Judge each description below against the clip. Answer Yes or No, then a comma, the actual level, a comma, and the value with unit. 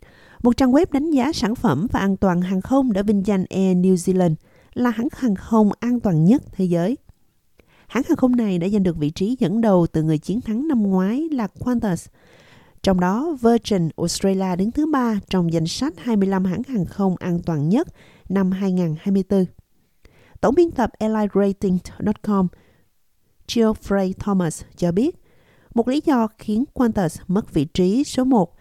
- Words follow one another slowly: No, average, 175 wpm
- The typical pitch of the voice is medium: No, high, 200 Hz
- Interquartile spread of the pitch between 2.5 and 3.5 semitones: No, average, 4.5 semitones